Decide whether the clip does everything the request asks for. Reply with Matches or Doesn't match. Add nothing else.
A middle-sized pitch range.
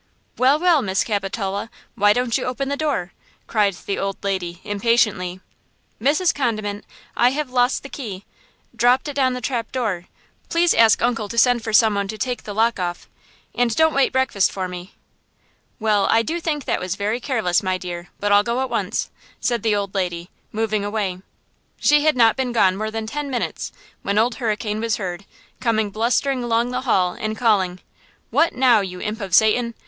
Matches